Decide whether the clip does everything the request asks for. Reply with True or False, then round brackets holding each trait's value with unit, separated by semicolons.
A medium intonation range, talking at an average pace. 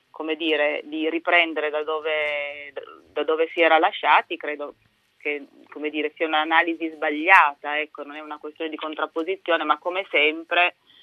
False (1.6 semitones; 150 wpm)